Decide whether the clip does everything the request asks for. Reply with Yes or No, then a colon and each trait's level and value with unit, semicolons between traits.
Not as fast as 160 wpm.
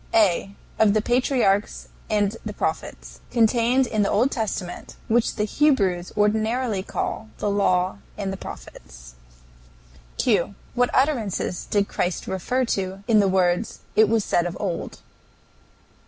Yes: average, 140 wpm